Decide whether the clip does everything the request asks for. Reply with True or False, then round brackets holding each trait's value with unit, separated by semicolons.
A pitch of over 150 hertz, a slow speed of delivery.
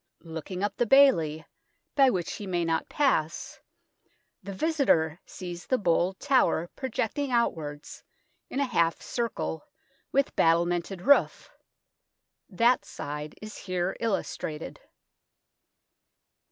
True (185 Hz; 110 wpm)